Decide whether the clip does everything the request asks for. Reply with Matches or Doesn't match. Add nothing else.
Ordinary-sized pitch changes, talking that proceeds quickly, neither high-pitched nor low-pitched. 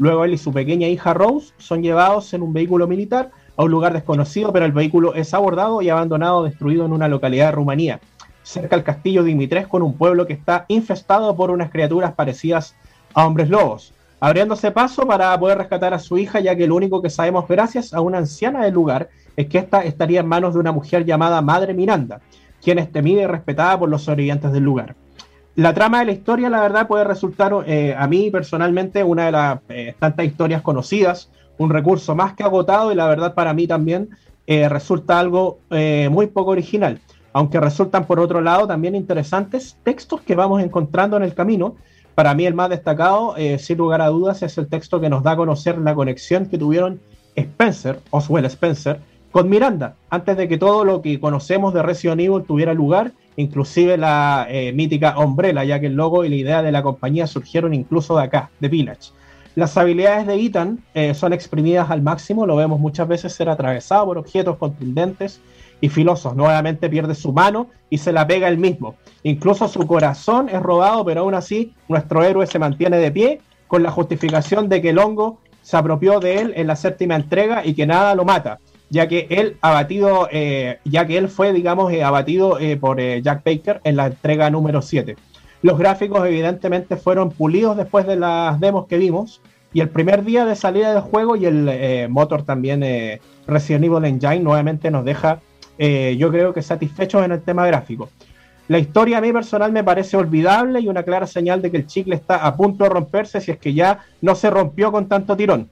Matches